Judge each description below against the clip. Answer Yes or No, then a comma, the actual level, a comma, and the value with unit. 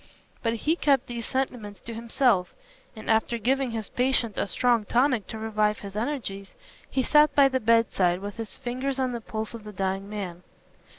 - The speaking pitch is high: Yes, high, 230 Hz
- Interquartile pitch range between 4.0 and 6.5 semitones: No, average, 3.6 semitones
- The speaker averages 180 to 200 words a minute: Yes, average, 185 wpm